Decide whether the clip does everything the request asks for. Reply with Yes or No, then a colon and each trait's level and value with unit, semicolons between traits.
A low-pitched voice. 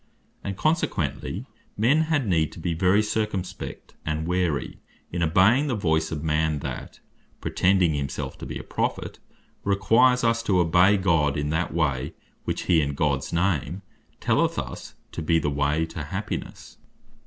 Yes: very low, 85 Hz